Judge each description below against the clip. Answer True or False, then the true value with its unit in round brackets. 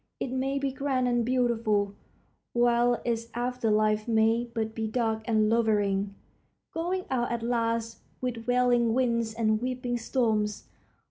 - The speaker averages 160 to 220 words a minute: False (140 wpm)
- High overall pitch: True (235 Hz)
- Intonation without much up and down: True (2.1 semitones)